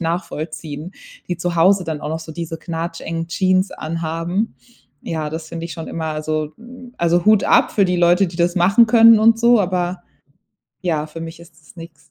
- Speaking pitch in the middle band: Yes, medium, 170 Hz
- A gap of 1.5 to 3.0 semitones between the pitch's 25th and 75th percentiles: Yes, narrow, 2.6 semitones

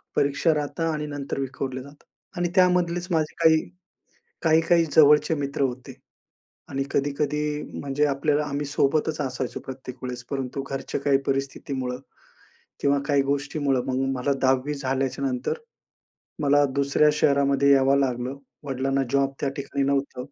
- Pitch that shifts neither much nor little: No, narrow, 1.7 semitones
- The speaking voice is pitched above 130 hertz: Yes, medium, 140 Hz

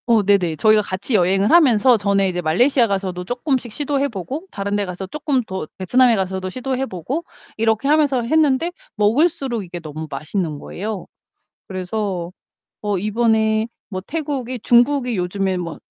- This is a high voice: Yes, high, 215 Hz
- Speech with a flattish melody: No, wide, 5.5 semitones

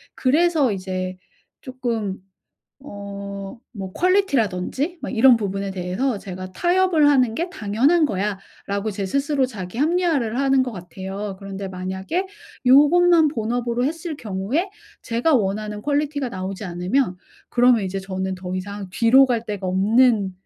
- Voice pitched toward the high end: Yes, high, 225 Hz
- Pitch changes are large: Yes, wide, 6.3 semitones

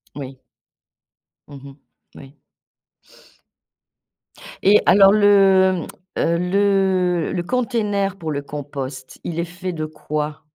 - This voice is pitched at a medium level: Yes, medium, 175 Hz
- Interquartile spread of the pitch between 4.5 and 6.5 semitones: Yes, average, 4.8 semitones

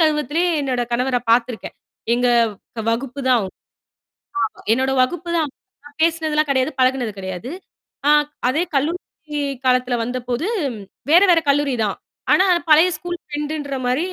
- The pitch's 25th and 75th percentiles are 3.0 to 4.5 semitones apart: Yes, average, 3.8 semitones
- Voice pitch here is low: No, very high, 270 Hz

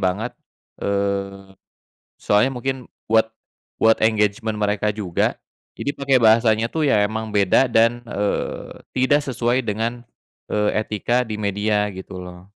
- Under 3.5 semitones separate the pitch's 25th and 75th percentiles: Yes, narrow, 2.5 semitones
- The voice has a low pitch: Yes, low, 110 Hz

